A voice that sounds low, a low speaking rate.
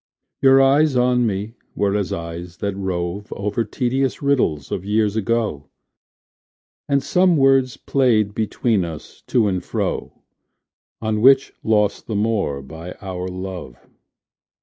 Yes: low, 105 Hz; slow, 130 wpm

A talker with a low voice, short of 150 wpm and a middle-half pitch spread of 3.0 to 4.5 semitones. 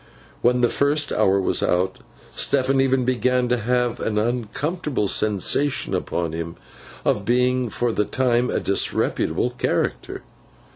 Yes: low, 120 Hz; slow, 135 wpm; average, 3.5 semitones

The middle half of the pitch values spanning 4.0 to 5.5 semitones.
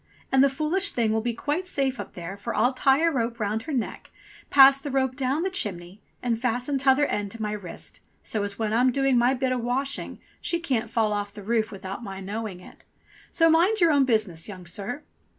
Yes: average, 4.6 semitones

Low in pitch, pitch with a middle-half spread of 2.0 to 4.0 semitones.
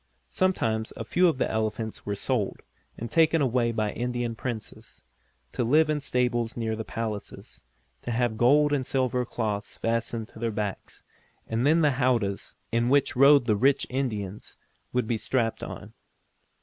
Yes: low, 120 Hz; average, 3.1 semitones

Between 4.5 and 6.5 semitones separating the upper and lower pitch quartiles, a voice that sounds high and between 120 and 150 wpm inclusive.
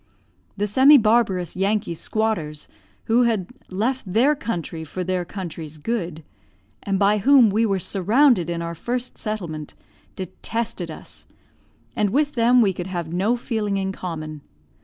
Yes: average, 4.8 semitones; high, 200 Hz; average, 145 wpm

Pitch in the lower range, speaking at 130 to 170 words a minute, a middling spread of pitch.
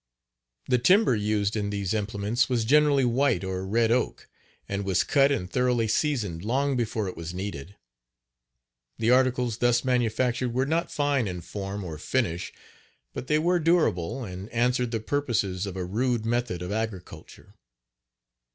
Yes: low, 115 Hz; average, 155 wpm; average, 4.4 semitones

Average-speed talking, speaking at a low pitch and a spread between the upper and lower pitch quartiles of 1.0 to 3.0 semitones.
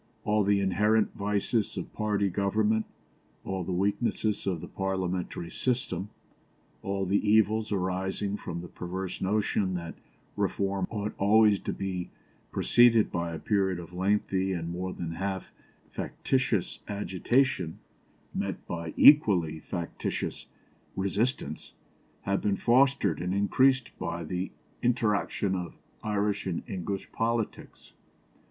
No: slow, 120 wpm; low, 100 Hz; average, 2.7 semitones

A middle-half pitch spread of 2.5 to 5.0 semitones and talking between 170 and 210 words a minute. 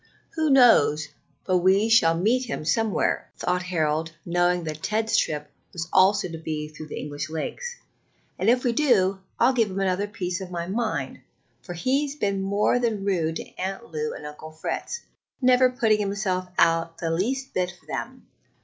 No: wide, 5.4 semitones; average, 175 wpm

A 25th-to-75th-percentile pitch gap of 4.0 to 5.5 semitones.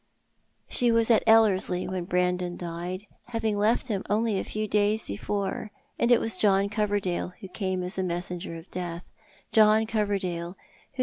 No: average, 3.2 semitones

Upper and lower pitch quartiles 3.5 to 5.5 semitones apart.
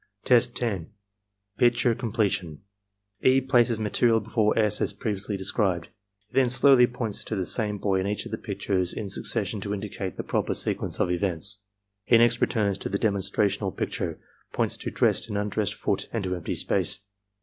No: average, 2.9 semitones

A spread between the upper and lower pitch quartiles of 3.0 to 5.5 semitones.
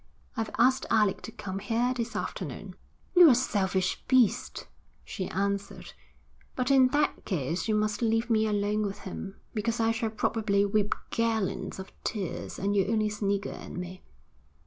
No: narrow, 2.5 semitones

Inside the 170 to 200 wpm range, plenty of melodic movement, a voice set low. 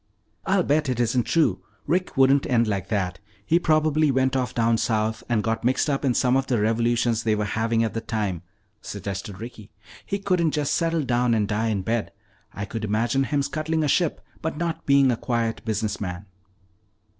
No: average, 195 wpm; average, 4.7 semitones; low, 120 Hz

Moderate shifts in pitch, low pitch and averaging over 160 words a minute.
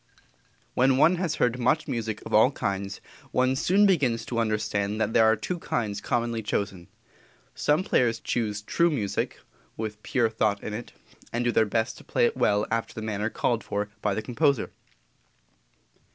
Yes: average, 3.6 semitones; low, 115 Hz; average, 175 wpm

